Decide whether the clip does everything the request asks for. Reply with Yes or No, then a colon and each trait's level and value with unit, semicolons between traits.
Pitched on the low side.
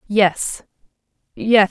No: high, 205 Hz